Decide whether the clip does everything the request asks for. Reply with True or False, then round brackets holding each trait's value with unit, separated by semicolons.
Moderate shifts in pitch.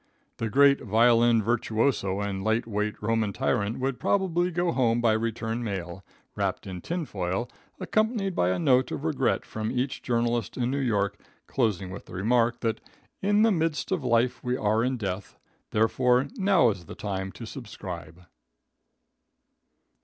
True (4.4 semitones)